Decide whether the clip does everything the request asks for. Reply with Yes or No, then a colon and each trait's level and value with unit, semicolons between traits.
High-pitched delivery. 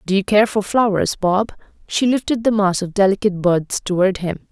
Yes: high, 200 Hz